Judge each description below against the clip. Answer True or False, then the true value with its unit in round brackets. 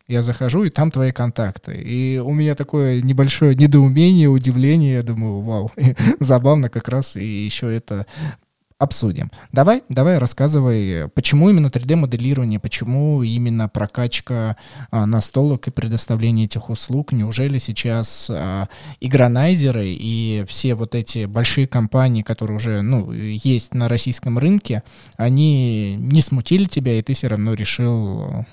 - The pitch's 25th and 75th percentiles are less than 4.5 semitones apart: True (3.5 semitones)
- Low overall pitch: True (125 Hz)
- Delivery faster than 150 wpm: False (135 wpm)